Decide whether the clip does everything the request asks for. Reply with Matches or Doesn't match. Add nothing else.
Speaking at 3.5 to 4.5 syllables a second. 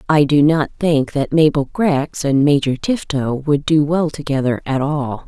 Matches